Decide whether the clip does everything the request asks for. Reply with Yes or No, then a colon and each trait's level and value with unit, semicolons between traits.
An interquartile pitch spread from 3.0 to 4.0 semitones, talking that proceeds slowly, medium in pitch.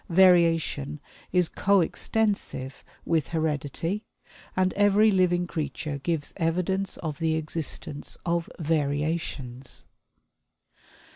Yes: average, 3.5 semitones; slow, 90 wpm; medium, 165 Hz